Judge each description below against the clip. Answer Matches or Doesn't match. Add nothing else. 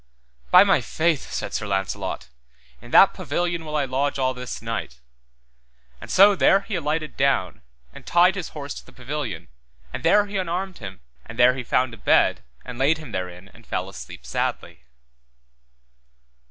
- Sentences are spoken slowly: Doesn't match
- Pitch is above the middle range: Doesn't match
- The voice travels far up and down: Matches